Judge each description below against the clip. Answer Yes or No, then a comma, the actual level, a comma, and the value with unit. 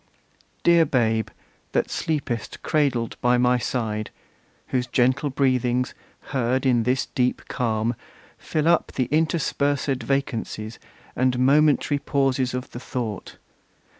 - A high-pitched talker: No, low, 130 Hz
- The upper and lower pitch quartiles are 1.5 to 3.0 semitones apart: Yes, narrow, 2.6 semitones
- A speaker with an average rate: No, slow, 115 wpm